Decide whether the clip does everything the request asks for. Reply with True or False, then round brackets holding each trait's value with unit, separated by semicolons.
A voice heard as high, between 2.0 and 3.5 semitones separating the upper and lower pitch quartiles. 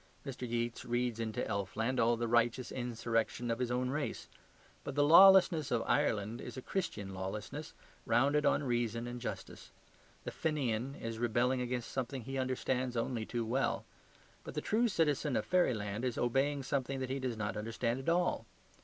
False (125 Hz; 2.8 semitones)